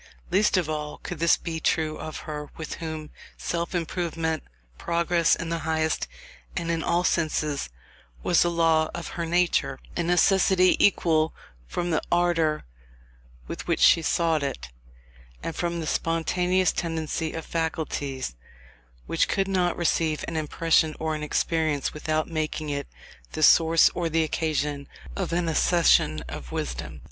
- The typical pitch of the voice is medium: Yes, medium, 160 Hz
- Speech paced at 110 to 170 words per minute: Yes, average, 150 wpm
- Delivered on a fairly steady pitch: Yes, narrow, 1.7 semitones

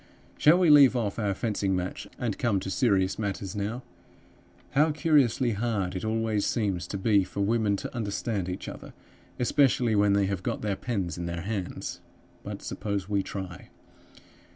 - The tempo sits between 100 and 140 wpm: No, average, 170 wpm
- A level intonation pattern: No, average, 3.5 semitones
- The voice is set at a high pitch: No, low, 105 Hz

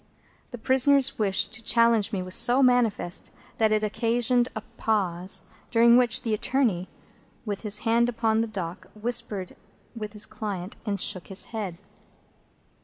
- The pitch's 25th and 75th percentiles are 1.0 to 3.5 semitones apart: Yes, average, 2.9 semitones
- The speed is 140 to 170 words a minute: Yes, average, 150 wpm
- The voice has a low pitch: No, high, 220 Hz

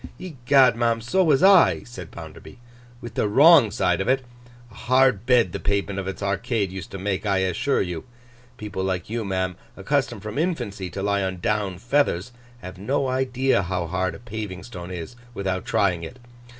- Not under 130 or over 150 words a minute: No, average, 185 wpm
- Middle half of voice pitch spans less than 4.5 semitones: No, average, 5.1 semitones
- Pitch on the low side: Yes, low, 100 Hz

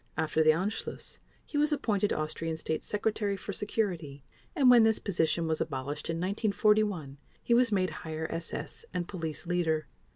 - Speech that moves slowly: No, average, 160 wpm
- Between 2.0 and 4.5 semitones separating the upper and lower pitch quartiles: No, average, 5.0 semitones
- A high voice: No, medium, 180 Hz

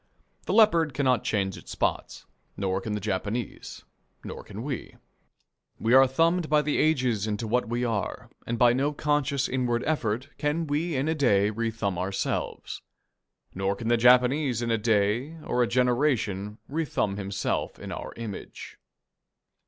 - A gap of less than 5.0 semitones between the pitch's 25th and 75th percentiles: No, average, 5.3 semitones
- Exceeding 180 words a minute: No, average, 155 wpm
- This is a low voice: Yes, low, 120 Hz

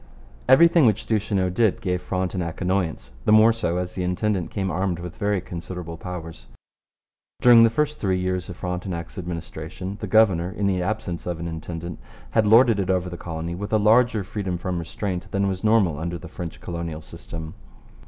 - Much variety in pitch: No, average, 3.2 semitones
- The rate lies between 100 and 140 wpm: No, average, 185 wpm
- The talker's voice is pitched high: No, very low, 90 Hz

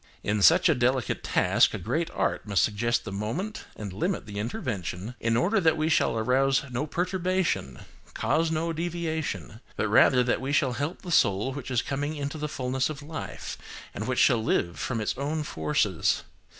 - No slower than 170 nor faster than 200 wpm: Yes, average, 185 wpm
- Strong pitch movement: Yes, wide, 6.3 semitones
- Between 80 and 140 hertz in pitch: Yes, low, 135 Hz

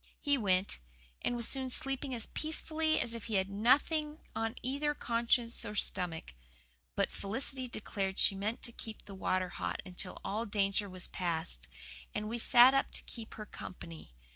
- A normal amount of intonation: Yes, average, 4.8 semitones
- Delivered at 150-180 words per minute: Yes, average, 170 wpm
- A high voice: Yes, high, 225 Hz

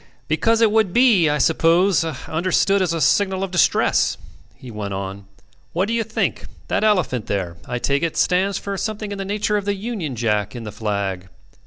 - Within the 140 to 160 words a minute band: No, average, 195 wpm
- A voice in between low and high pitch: Yes, medium, 175 Hz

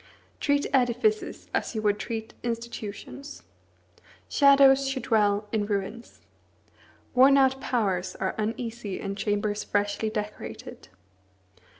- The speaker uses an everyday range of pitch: Yes, average, 4.2 semitones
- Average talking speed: No, slow, 105 wpm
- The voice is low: No, high, 220 Hz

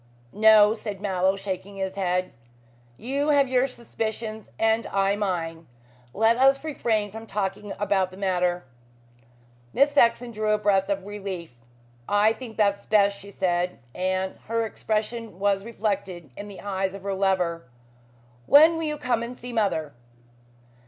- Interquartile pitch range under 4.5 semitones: Yes, average, 2.9 semitones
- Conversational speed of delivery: Yes, average, 150 wpm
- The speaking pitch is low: No, high, 205 Hz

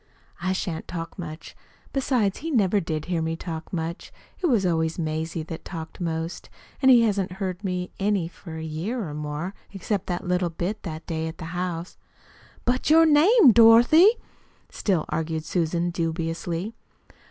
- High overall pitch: No, medium, 175 Hz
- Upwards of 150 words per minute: Yes, average, 165 wpm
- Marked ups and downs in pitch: No, average, 4.2 semitones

